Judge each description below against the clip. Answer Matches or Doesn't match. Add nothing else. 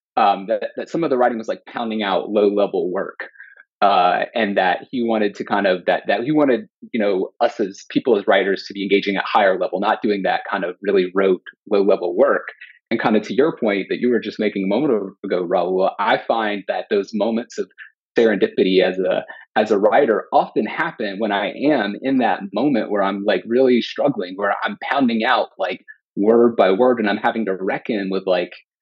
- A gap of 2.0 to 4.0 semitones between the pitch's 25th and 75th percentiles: Matches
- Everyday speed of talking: Doesn't match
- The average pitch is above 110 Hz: Doesn't match